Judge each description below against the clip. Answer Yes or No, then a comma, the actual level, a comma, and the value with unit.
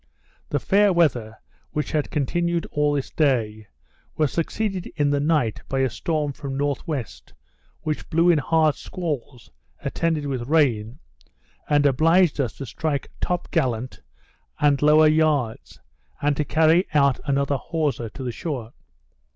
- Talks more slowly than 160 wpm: Yes, average, 145 wpm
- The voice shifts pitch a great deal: No, average, 3.3 semitones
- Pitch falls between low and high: Yes, medium, 145 Hz